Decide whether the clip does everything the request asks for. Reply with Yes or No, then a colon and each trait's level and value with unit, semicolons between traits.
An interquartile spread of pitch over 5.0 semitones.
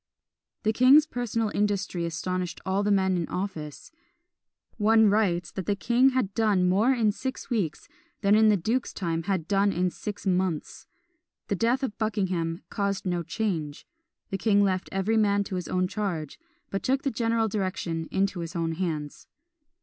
No: average, 3.5 semitones